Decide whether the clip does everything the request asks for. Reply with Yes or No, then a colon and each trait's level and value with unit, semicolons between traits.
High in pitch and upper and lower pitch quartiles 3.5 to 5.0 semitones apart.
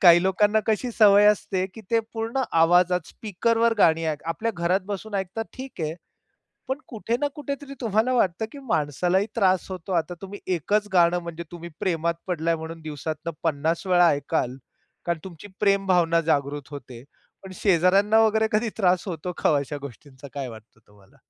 No: medium, 180 Hz; average, 4.5 semitones